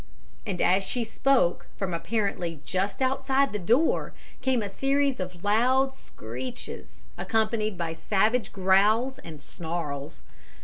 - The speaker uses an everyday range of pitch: No, wide, 6.5 semitones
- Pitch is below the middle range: No, high, 200 Hz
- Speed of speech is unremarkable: No, slow, 125 wpm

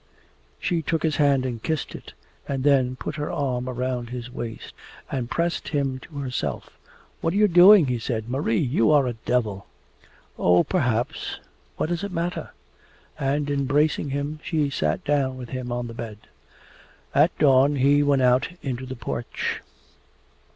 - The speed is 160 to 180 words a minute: Yes, average, 165 wpm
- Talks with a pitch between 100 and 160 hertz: Yes, low, 135 Hz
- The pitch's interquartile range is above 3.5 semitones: No, average, 3.2 semitones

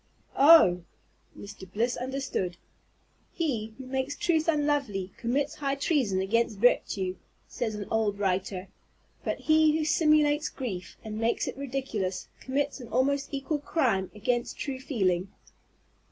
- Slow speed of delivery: Yes, slow, 130 wpm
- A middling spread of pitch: No, wide, 6.1 semitones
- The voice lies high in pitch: Yes, very high, 250 Hz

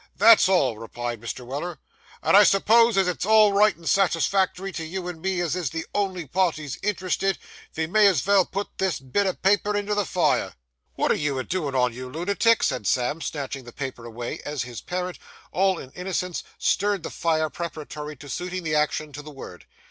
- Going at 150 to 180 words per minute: No, average, 200 wpm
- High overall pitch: No, medium, 170 Hz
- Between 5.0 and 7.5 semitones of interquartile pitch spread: Yes, wide, 5.4 semitones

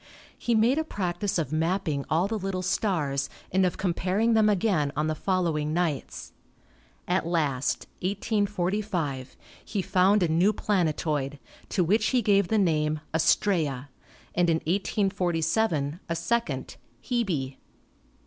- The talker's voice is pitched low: No, medium, 180 Hz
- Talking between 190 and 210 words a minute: No, slow, 135 wpm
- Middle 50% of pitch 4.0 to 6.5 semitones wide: Yes, average, 4.6 semitones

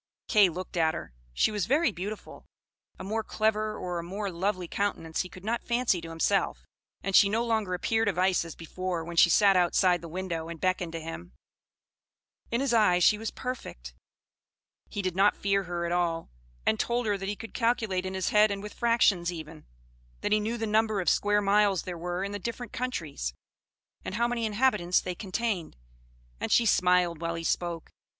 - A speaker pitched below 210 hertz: Yes, high, 190 Hz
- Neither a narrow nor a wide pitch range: Yes, average, 3.8 semitones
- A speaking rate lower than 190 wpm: No, average, 200 wpm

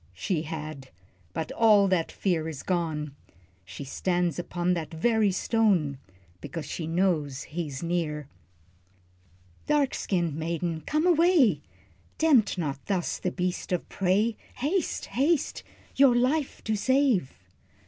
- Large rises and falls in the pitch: Yes, wide, 6.2 semitones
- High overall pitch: No, medium, 180 Hz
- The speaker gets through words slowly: Yes, slow, 125 wpm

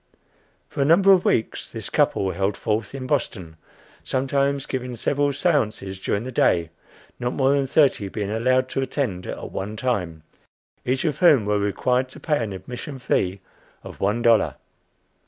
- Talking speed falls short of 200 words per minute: Yes, average, 165 wpm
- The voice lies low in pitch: Yes, low, 125 Hz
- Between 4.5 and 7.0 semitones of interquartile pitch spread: Yes, average, 5.2 semitones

